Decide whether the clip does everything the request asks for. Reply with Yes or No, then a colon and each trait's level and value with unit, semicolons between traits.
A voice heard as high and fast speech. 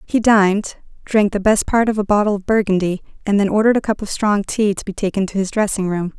Yes: high, 205 Hz; fast, 250 wpm